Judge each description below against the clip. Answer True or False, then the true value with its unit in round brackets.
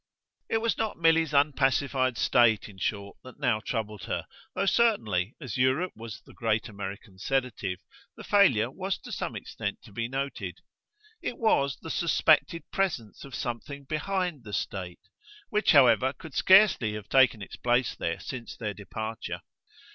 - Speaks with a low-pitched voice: True (130 Hz)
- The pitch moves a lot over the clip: True (6.7 semitones)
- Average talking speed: True (155 wpm)